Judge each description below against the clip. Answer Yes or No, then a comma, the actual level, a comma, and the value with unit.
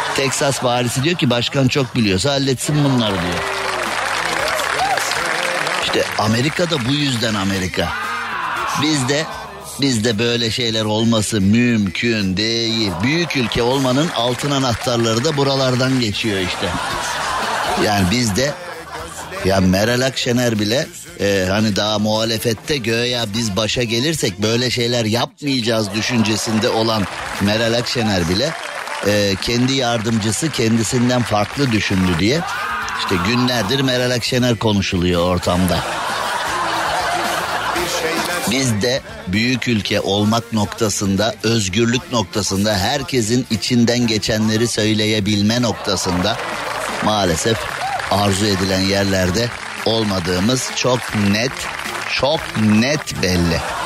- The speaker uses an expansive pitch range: No, average, 3.2 semitones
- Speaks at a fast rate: No, average, 105 wpm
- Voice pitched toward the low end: Yes, low, 115 Hz